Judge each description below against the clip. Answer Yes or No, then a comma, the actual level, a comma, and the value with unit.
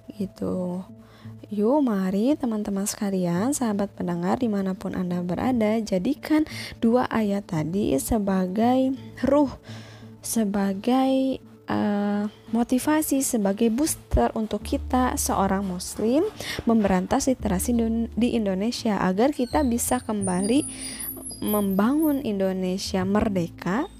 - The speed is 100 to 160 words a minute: No, average, 90 wpm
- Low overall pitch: No, high, 215 Hz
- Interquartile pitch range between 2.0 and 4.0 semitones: No, average, 4.9 semitones